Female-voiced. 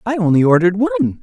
Yes: female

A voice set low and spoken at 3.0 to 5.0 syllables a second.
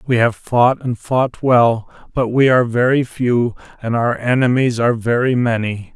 Yes: low, 120 Hz; 4.5 syllables/s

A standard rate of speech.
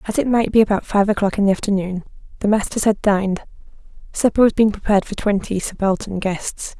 Yes: average, 195 wpm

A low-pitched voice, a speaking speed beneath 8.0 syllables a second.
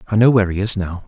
No: low, 100 Hz; 8.2 syllables/s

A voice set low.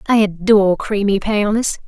No: high, 205 Hz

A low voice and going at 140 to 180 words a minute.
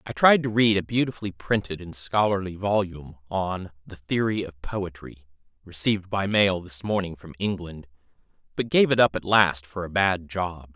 Yes: very low, 95 Hz; average, 175 wpm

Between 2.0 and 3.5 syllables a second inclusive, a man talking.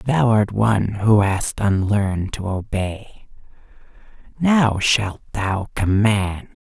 Yes: 3.4 syllables/s; male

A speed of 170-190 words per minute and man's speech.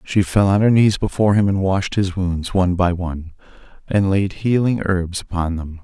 No: fast, 205 wpm; male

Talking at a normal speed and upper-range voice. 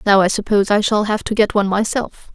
No: fast, 255 wpm; high, 205 Hz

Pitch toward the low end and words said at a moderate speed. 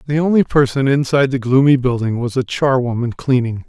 Yes: low, 130 Hz; average, 180 wpm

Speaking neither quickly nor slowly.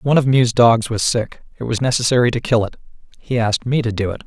No: fast, 255 wpm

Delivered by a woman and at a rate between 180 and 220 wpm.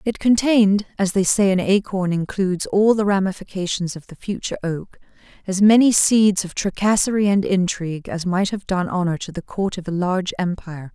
Yes: female; average, 185 wpm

